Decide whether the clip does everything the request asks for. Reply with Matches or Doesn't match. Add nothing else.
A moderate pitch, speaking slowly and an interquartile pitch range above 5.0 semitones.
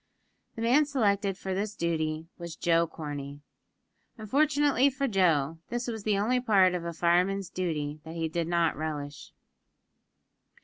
Doesn't match